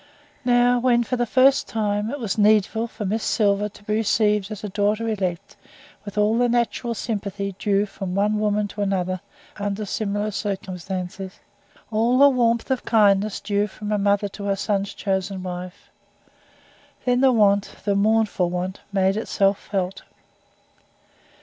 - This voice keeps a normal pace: Yes, average, 155 wpm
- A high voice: Yes, high, 205 Hz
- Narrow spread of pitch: Yes, narrow, 2.2 semitones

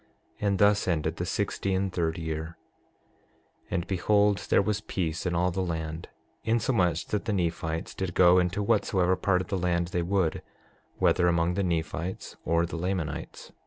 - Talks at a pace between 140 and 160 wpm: No, average, 170 wpm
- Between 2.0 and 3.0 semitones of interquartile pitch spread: Yes, narrow, 2.5 semitones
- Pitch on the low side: Yes, very low, 90 Hz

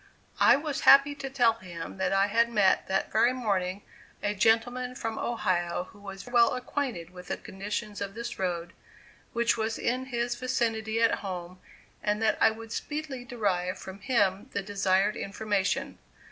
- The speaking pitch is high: Yes, high, 220 Hz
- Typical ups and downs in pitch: Yes, average, 3.8 semitones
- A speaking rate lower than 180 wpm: Yes, average, 165 wpm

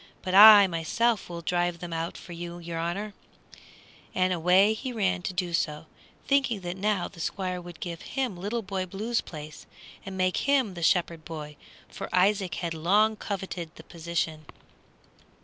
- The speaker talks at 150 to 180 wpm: Yes, average, 165 wpm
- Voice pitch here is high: No, medium, 180 Hz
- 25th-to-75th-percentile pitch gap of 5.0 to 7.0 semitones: No, average, 3.1 semitones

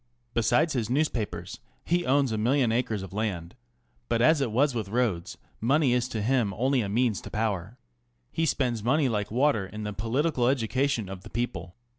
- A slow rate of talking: No, average, 185 wpm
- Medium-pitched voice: No, low, 115 Hz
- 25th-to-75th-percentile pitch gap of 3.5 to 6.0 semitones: Yes, average, 4.2 semitones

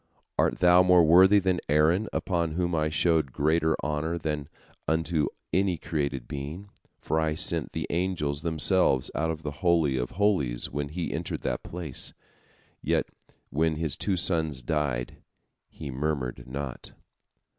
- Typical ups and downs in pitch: Yes, average, 3.2 semitones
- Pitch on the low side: Yes, very low, 80 Hz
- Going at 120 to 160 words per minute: Yes, average, 145 wpm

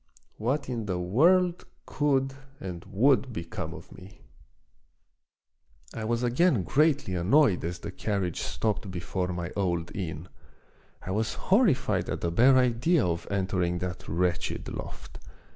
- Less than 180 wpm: Yes, slow, 135 wpm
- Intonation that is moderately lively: No, wide, 6.9 semitones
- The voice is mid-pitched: No, low, 100 Hz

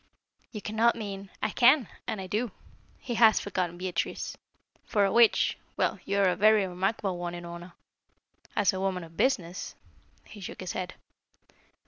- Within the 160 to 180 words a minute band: Yes, average, 170 wpm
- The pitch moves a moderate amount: Yes, average, 3.2 semitones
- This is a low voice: No, high, 195 Hz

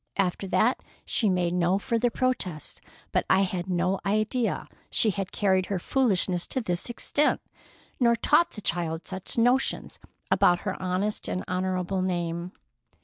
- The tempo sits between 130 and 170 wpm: Yes, average, 145 wpm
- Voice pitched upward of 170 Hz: Yes, high, 190 Hz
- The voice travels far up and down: No, average, 3.7 semitones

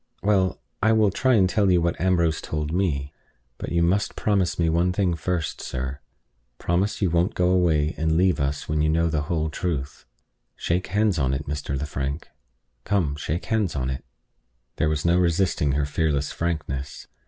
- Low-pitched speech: Yes, very low, 85 Hz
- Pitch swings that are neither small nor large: Yes, average, 3.8 semitones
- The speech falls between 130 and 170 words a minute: No, average, 180 wpm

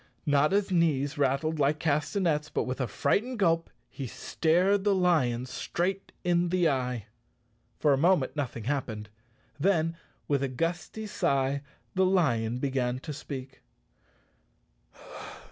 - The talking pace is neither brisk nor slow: No, slow, 130 wpm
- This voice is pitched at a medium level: Yes, medium, 150 Hz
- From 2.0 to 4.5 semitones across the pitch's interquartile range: No, average, 5.0 semitones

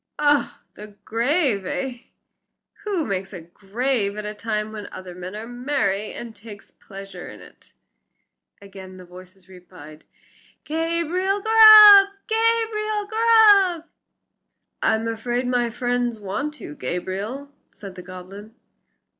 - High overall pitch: Yes, high, 230 Hz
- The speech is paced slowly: Yes, slow, 120 wpm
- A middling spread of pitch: No, wide, 8.8 semitones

